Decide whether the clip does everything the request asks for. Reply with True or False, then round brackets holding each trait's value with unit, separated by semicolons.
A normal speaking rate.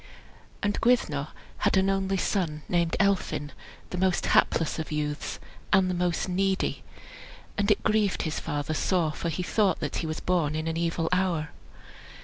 True (165 wpm)